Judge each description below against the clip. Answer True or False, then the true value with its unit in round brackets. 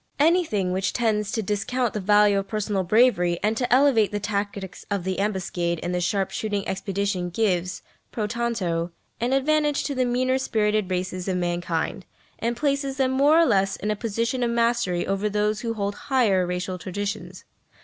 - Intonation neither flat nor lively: True (4.0 semitones)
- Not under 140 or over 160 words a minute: False (180 wpm)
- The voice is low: False (210 Hz)